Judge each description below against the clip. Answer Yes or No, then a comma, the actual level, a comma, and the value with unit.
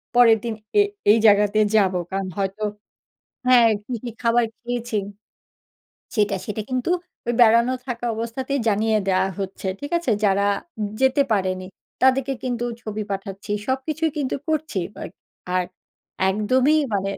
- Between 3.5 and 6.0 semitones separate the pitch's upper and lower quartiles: Yes, average, 4.2 semitones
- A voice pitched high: Yes, high, 230 Hz